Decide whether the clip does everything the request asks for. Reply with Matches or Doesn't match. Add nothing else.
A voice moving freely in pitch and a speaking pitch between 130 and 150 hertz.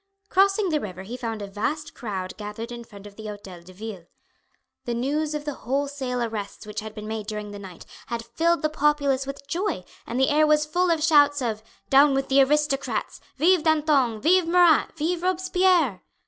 Doesn't match